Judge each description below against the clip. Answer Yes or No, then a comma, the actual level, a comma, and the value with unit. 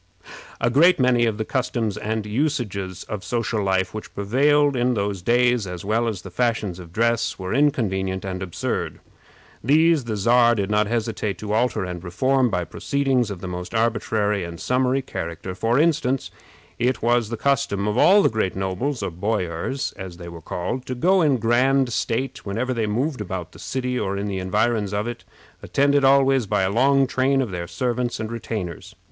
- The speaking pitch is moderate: No, low, 115 Hz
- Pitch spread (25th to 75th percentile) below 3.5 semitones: No, average, 4.9 semitones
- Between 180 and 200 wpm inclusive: Yes, average, 190 wpm